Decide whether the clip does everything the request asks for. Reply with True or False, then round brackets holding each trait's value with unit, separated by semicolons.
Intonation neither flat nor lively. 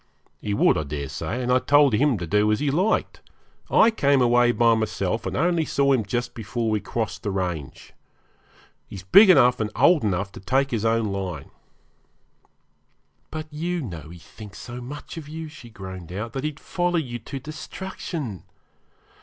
False (6.2 semitones)